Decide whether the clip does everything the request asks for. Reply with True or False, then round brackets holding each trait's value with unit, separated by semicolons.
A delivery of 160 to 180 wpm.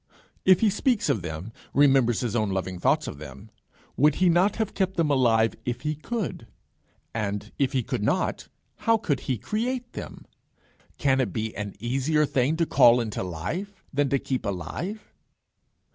True (175 wpm)